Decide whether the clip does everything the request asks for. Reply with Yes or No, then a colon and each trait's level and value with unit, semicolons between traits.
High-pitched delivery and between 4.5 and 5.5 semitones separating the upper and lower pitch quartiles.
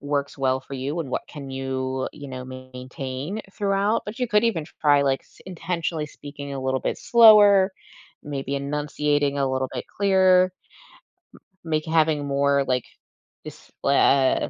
No: medium, 145 Hz; average, 5.0 semitones